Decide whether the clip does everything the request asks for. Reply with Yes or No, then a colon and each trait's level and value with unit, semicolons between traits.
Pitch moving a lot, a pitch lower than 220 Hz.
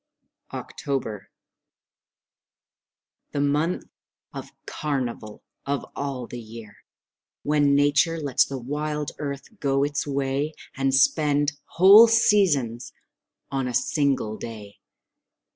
No: average, 2.9 semitones; medium, 140 Hz